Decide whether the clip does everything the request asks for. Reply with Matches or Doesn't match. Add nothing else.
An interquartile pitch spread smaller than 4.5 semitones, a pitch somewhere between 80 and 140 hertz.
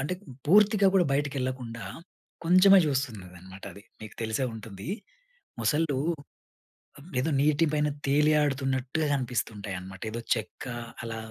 Doesn't match